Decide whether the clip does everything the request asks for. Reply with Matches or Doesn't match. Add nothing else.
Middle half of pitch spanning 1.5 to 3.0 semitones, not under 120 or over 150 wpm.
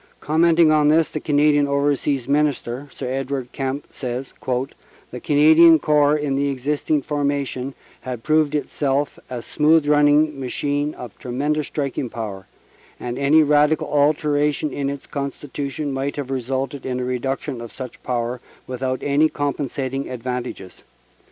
Matches